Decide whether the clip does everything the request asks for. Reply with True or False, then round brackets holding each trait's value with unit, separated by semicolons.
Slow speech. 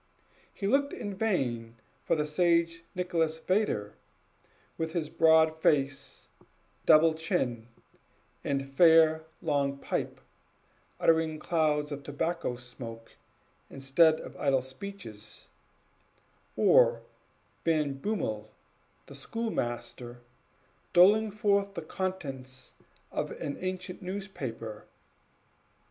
True (95 wpm)